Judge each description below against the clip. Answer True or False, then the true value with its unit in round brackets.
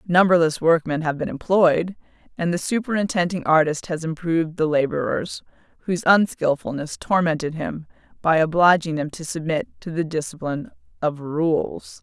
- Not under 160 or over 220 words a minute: False (135 wpm)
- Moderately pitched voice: True (165 Hz)